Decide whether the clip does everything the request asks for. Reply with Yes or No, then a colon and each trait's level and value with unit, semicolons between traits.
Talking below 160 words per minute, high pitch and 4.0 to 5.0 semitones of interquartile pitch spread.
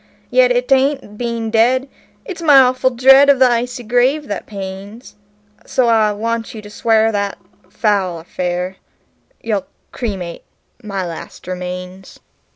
Yes: average, 140 wpm; high, 225 Hz; average, 4.7 semitones